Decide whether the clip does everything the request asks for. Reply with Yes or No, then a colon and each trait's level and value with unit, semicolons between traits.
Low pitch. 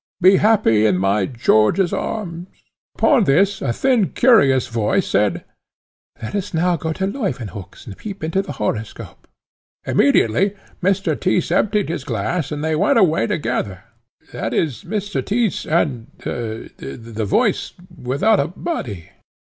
No: medium, 160 Hz